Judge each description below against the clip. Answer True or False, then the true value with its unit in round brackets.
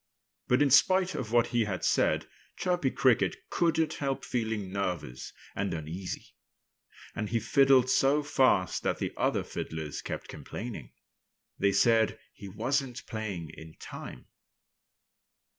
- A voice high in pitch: False (115 Hz)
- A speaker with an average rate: False (130 wpm)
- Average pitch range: False (5.8 semitones)